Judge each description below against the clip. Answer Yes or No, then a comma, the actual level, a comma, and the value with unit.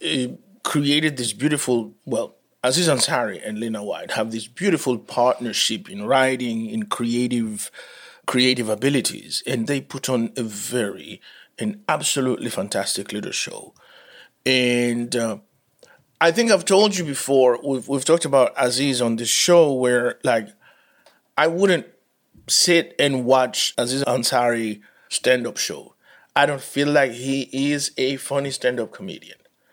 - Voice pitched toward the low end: Yes, low, 130 Hz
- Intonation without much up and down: No, average, 3.4 semitones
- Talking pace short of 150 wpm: Yes, slow, 135 wpm